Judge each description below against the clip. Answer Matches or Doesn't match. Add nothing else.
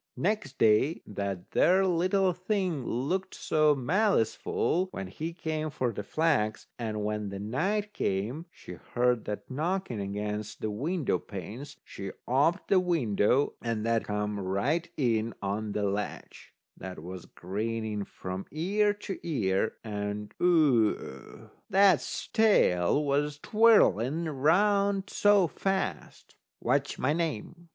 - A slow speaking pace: Matches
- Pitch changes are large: Matches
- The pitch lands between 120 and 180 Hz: Matches